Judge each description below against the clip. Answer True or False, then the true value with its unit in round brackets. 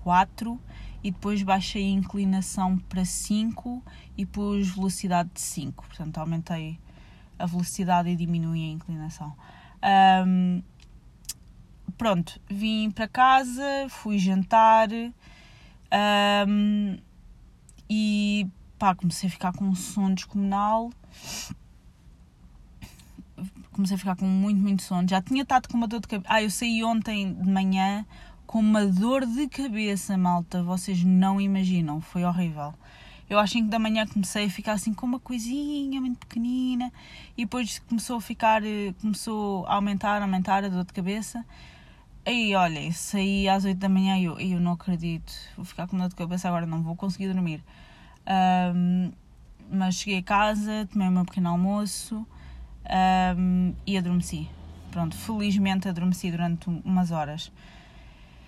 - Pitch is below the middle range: False (190 Hz)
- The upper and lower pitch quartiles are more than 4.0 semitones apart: False (3.1 semitones)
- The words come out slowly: False (145 wpm)